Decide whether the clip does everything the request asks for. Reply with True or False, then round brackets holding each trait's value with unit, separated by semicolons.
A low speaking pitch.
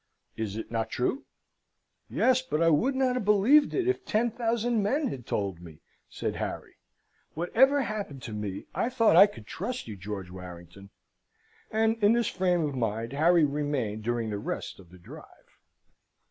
False (160 Hz)